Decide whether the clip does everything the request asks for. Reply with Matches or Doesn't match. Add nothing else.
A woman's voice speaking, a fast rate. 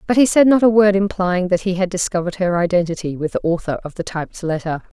Matches